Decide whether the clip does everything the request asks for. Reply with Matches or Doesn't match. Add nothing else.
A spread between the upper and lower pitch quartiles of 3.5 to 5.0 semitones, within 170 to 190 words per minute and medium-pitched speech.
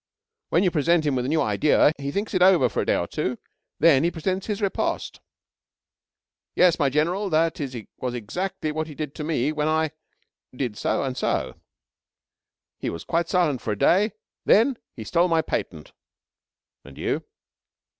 Matches